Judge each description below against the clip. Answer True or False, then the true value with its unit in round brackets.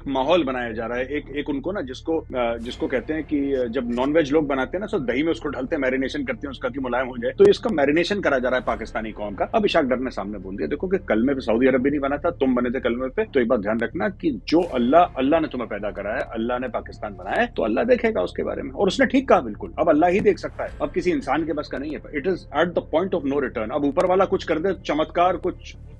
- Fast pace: True (285 wpm)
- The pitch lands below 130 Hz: False (140 Hz)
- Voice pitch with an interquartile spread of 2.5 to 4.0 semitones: False (5.6 semitones)